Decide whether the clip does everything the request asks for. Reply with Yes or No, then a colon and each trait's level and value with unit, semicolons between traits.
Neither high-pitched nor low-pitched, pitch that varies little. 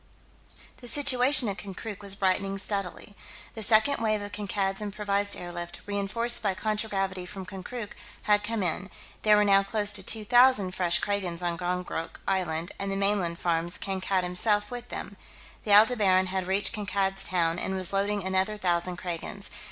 No: high, 195 Hz; narrow, 2.1 semitones